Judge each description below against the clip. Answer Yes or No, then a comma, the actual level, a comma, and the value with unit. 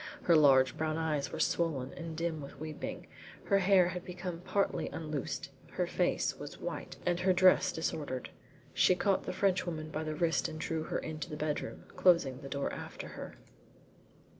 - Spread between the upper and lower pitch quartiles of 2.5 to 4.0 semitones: Yes, average, 2.8 semitones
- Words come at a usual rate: Yes, average, 175 wpm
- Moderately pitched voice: Yes, medium, 160 Hz